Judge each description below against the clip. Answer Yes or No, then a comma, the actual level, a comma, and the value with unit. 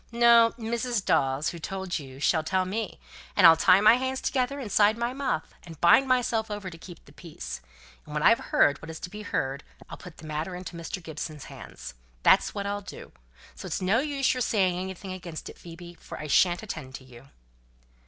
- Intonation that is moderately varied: No, wide, 5.8 semitones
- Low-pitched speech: No, medium, 185 Hz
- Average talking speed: No, fast, 210 wpm